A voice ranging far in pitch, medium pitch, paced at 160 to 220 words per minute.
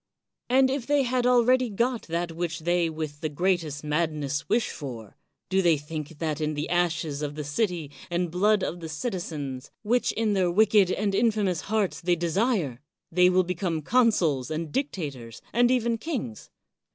Yes: wide, 6.1 semitones; medium, 175 Hz; average, 170 wpm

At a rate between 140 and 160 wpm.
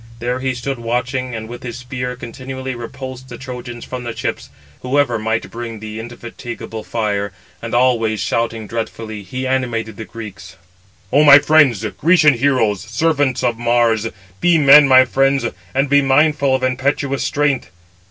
Yes: average, 155 wpm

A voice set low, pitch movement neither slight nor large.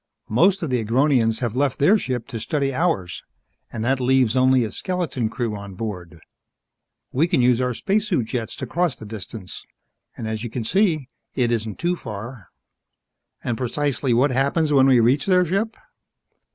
Yes: low, 125 Hz; average, 4.5 semitones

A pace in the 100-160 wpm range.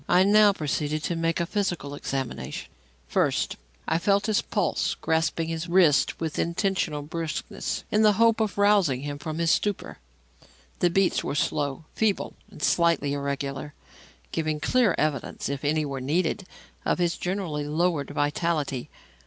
Yes: average, 150 wpm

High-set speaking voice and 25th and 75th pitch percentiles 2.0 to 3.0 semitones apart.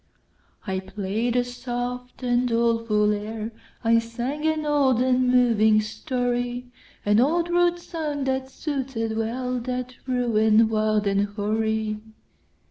Yes: high, 240 Hz; average, 2.7 semitones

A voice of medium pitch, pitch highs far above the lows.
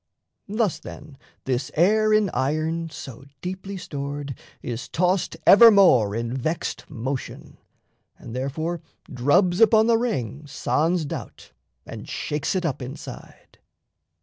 Yes: medium, 155 Hz; wide, 6.1 semitones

